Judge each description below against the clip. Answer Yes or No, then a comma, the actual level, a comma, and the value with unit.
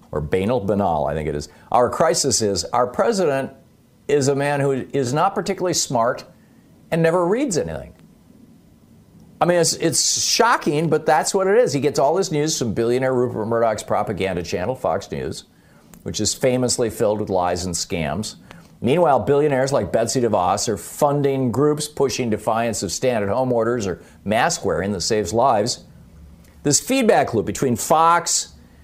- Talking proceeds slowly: No, average, 165 wpm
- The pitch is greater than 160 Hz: No, low, 130 Hz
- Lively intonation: Yes, wide, 6.6 semitones